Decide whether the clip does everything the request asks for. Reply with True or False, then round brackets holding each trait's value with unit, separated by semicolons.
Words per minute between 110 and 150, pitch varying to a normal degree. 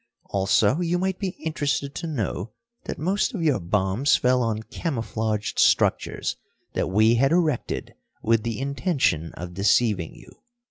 False (145 wpm; 7.1 semitones)